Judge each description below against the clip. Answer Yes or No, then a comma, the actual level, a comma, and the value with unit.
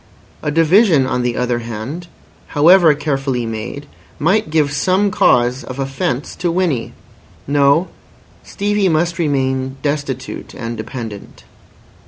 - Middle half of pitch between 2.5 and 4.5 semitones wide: No, average, 5.1 semitones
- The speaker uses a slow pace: Yes, slow, 120 wpm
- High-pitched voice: No, medium, 145 Hz